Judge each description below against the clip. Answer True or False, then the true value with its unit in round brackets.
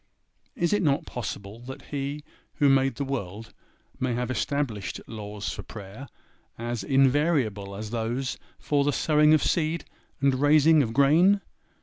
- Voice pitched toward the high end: False (135 Hz)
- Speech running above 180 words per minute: False (145 wpm)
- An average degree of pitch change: True (4.6 semitones)